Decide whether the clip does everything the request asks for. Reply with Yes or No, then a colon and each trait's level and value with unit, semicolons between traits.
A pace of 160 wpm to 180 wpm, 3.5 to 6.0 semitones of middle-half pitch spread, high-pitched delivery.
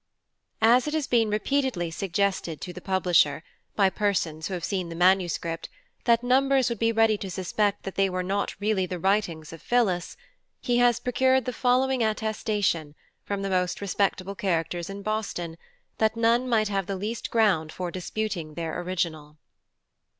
Yes: average, 165 wpm; average, 4.1 semitones; high, 200 Hz